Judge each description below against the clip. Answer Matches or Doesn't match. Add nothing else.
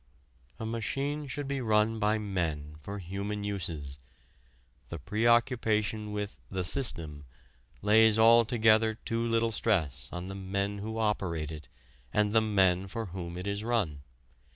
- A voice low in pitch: Matches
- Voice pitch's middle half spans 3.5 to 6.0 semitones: Matches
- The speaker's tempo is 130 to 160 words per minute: Matches